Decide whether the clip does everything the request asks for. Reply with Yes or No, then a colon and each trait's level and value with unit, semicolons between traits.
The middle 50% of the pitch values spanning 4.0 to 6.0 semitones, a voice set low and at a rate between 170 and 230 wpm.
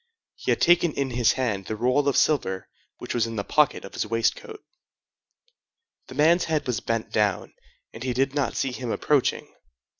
Yes: average, 4.5 semitones; low, 125 Hz; average, 185 wpm